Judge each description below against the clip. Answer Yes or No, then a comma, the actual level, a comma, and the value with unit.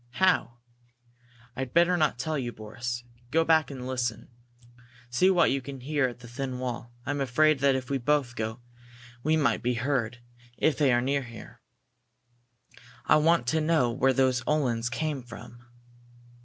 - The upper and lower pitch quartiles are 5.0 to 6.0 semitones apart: No, average, 3.9 semitones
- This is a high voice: No, low, 130 Hz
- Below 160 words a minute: No, average, 165 wpm